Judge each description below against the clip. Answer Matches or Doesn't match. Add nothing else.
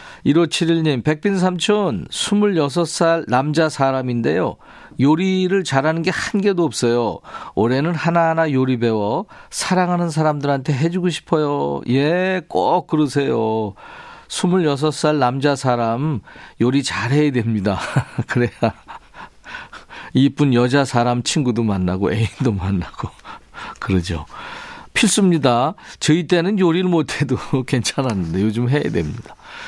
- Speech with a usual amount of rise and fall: Doesn't match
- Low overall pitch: Doesn't match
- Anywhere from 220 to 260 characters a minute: Matches